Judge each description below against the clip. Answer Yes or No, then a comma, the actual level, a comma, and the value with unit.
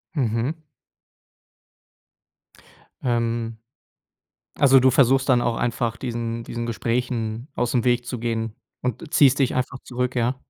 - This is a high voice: No, low, 120 Hz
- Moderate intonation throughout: No, narrow, 1.8 semitones